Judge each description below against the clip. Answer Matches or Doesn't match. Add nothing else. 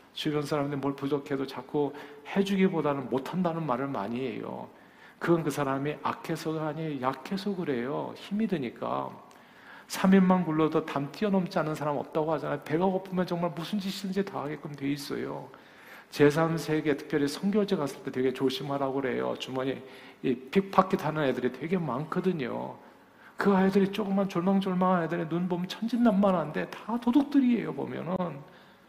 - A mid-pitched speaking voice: Matches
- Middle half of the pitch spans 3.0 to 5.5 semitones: Matches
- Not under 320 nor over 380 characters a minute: Matches